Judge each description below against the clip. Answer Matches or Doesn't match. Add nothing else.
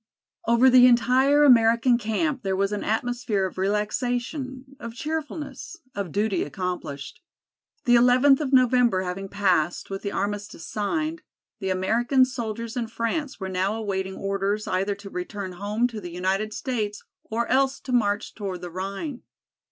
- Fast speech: Doesn't match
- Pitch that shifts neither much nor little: Matches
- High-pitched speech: Matches